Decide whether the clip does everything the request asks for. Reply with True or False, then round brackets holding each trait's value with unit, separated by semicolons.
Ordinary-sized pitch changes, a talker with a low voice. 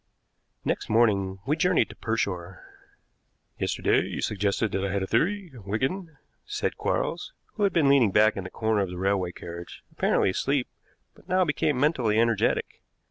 False (7.2 semitones; 110 Hz)